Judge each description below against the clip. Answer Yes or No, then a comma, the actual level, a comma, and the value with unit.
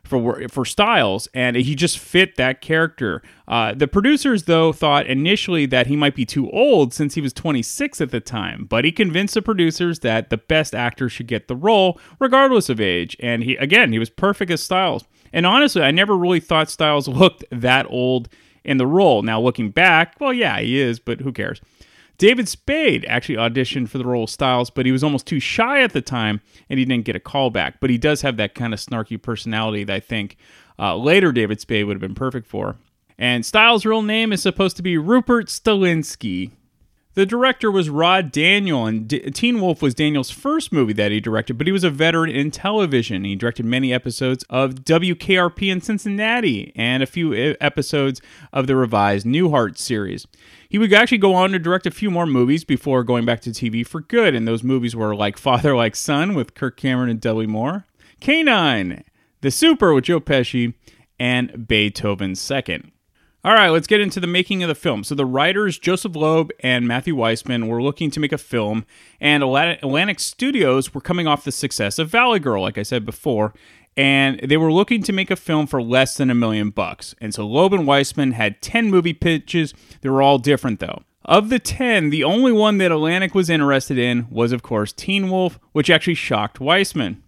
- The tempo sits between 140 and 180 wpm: No, fast, 205 wpm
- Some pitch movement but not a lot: No, wide, 7.0 semitones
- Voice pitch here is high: No, medium, 140 Hz